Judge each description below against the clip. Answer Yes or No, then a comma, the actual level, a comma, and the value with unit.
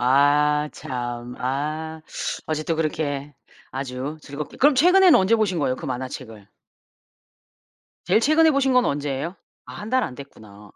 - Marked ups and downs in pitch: Yes, wide, 6.7 semitones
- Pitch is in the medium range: Yes, medium, 150 Hz